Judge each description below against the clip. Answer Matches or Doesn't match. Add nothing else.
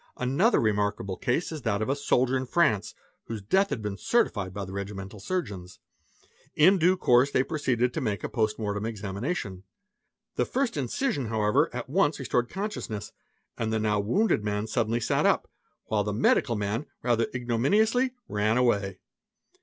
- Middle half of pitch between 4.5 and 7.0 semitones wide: Matches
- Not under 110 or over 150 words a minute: Matches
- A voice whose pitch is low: Matches